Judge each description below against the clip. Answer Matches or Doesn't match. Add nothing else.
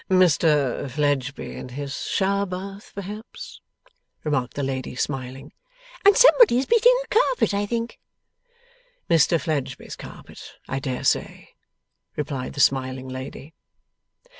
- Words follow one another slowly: Matches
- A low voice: Doesn't match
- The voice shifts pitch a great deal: Matches